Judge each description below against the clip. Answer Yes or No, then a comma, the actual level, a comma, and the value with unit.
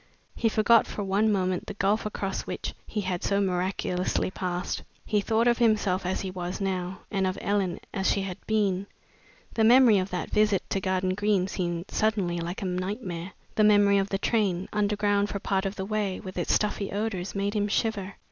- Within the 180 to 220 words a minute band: Yes, average, 195 wpm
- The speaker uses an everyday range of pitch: No, narrow, 2.2 semitones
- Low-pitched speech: No, high, 195 Hz